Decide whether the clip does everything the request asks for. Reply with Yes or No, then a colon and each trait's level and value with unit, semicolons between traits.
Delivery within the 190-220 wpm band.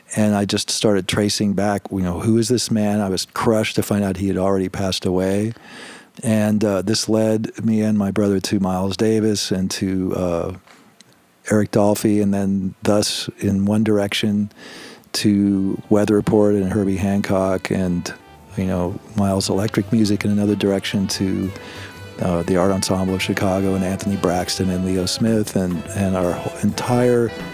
No: average, 170 wpm